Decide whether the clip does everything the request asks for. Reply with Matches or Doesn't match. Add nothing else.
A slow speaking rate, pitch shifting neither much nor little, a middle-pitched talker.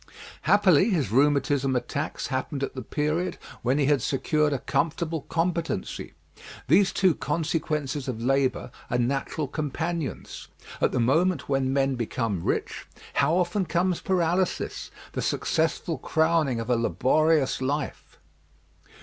Matches